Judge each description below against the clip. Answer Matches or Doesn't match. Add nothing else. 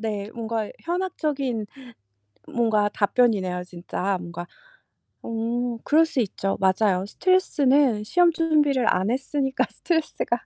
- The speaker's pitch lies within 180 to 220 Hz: Doesn't match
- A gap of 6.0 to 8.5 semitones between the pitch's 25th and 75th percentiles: Doesn't match